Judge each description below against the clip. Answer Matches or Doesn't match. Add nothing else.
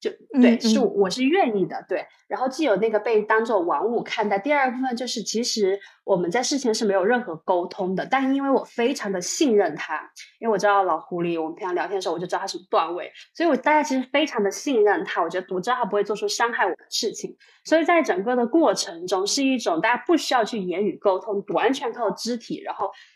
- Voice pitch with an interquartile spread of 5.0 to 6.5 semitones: Matches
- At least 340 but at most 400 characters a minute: Matches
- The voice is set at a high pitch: Matches